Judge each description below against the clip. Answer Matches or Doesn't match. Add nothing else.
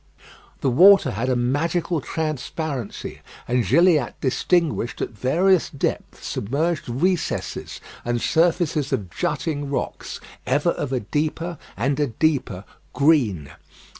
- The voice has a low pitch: Doesn't match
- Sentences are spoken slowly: Matches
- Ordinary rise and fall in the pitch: Matches